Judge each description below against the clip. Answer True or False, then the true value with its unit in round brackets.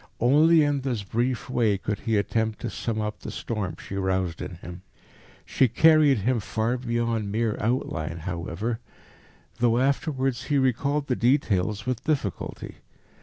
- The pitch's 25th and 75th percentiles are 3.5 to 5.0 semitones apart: True (4.4 semitones)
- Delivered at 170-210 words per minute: False (150 wpm)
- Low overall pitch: True (115 Hz)